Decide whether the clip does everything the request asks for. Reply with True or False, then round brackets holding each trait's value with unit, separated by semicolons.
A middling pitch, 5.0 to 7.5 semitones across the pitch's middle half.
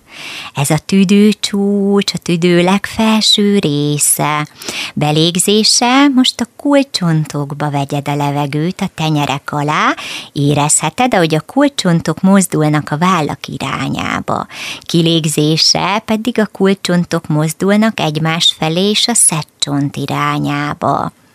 True (170 Hz; 5.3 semitones)